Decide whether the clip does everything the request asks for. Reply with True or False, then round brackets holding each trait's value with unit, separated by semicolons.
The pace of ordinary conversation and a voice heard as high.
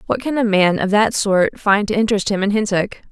False (250 wpm; 205 Hz)